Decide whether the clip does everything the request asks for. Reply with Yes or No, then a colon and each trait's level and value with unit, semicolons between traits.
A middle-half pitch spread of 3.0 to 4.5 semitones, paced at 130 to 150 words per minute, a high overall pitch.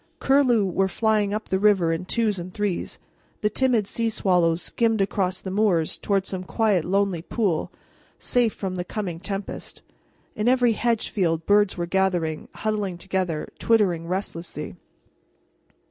Yes: average, 3.3 semitones; average, 145 wpm; high, 195 Hz